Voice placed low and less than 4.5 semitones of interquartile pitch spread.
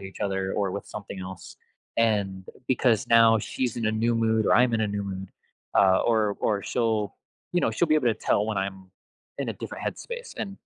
Yes: low, 110 Hz; average, 2.9 semitones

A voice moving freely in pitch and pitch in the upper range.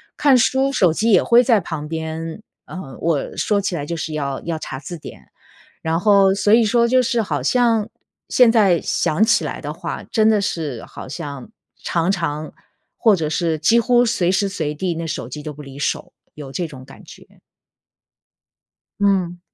No: wide, 5.9 semitones; medium, 175 Hz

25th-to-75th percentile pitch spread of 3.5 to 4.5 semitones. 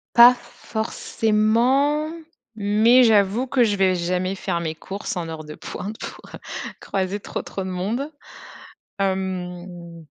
Yes: average, 3.9 semitones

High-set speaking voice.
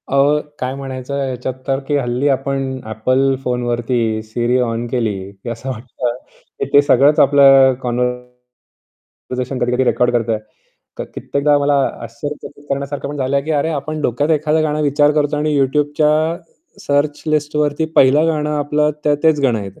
No: medium, 140 Hz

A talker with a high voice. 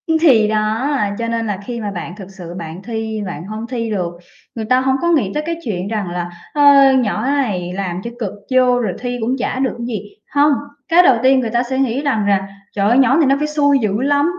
Yes: high, 235 Hz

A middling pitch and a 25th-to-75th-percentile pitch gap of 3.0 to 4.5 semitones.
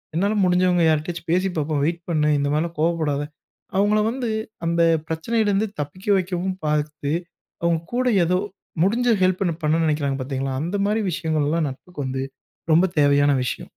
Yes: medium, 165 Hz; average, 3.8 semitones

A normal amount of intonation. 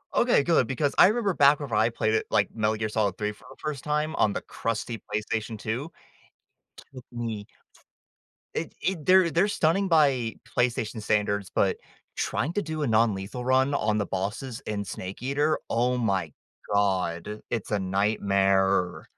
No: wide, 5.8 semitones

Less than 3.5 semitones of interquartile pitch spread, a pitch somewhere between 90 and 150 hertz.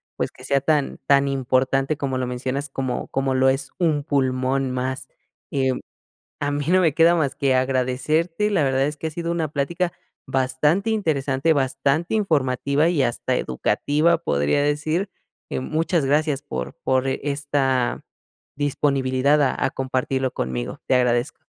Yes: average, 2.8 semitones; medium, 140 Hz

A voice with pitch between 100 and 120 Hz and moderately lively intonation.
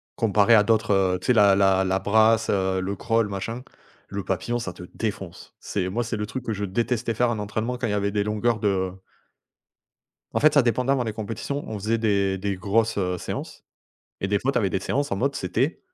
Yes: low, 105 Hz; average, 3.0 semitones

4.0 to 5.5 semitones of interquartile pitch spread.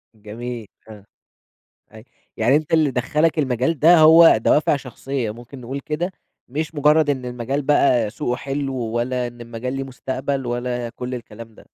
No: average, 3.5 semitones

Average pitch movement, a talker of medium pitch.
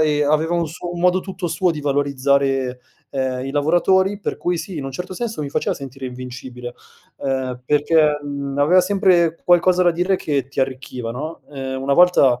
Yes: average, 4.6 semitones; medium, 145 Hz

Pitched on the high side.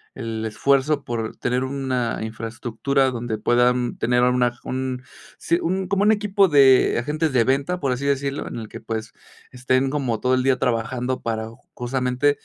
No: low, 130 Hz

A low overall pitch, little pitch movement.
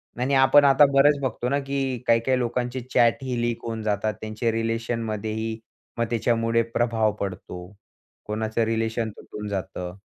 Yes: low, 115 Hz; narrow, 2.2 semitones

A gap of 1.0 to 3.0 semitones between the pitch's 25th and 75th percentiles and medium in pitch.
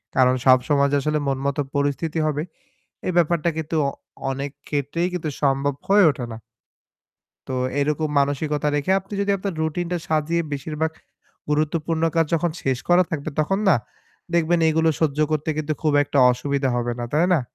Yes: average, 2.7 semitones; medium, 150 Hz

